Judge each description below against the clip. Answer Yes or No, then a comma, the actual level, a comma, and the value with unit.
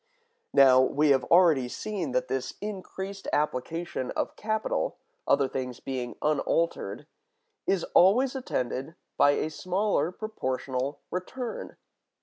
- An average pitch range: No, wide, 6.6 semitones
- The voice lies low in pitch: No, medium, 155 Hz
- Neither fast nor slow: No, slow, 115 wpm